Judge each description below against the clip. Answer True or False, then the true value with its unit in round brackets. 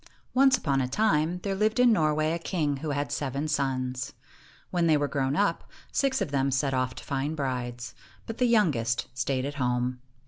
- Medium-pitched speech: True (145 Hz)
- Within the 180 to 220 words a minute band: True (195 wpm)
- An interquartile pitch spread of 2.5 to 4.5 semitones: False (4.9 semitones)